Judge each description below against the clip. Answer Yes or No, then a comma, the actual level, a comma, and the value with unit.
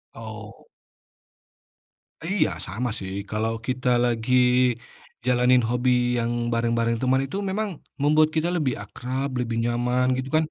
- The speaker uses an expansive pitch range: No, narrow, 2.4 semitones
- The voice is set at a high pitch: No, low, 125 Hz